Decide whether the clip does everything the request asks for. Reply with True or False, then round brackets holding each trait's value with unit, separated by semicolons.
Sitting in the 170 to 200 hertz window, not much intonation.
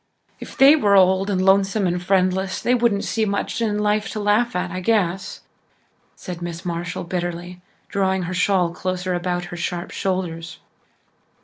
True (185 Hz; 2.3 semitones)